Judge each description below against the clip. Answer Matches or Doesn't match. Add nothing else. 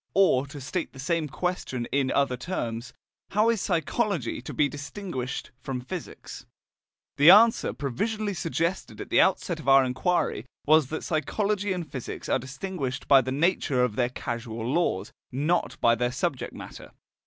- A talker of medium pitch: Matches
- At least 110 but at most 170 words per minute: Matches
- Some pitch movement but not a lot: Doesn't match